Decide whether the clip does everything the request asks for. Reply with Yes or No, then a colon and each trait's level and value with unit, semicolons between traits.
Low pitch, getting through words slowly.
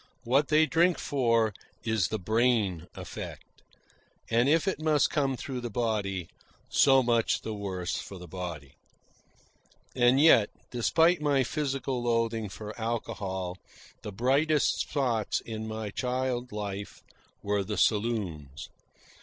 Yes: low, 115 Hz; slow, 130 wpm